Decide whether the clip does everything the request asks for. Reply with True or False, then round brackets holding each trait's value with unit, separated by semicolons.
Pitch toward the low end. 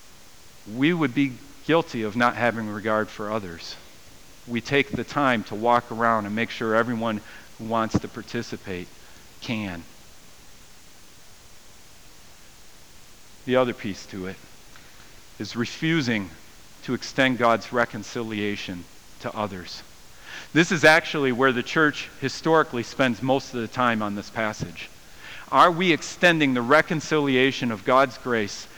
True (120 Hz)